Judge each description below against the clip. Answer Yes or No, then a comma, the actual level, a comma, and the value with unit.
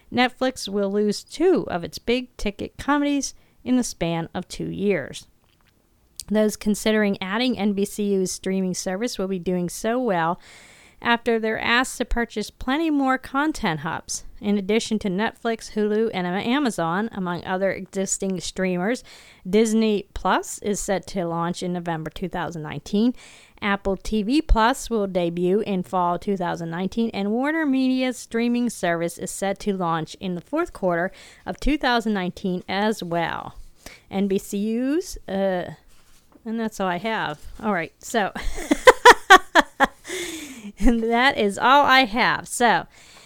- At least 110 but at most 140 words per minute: Yes, slow, 135 wpm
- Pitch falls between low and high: No, high, 210 Hz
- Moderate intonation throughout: Yes, average, 4.7 semitones